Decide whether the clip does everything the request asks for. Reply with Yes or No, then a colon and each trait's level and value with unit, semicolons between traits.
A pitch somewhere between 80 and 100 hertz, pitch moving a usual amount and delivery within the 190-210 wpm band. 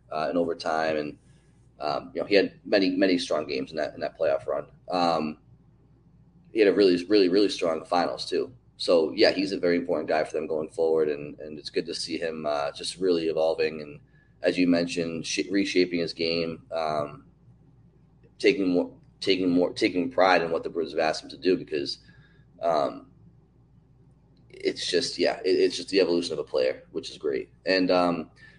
Yes: very low, 85 Hz; average, 3.6 semitones; average, 195 wpm